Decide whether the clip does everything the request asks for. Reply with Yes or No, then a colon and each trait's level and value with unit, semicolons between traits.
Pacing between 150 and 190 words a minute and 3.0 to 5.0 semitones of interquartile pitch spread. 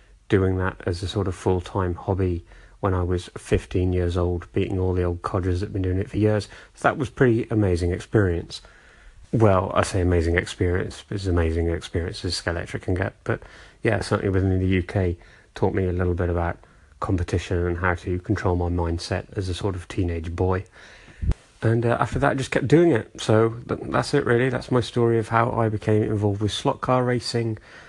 No: average, 200 wpm; average, 3.3 semitones